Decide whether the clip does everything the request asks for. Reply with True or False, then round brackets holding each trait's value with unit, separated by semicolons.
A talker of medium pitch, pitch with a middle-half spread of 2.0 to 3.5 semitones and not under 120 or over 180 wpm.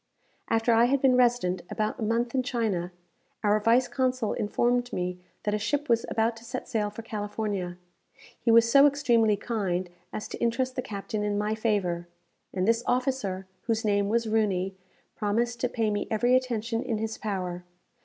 False (225 Hz; 2.8 semitones; 175 wpm)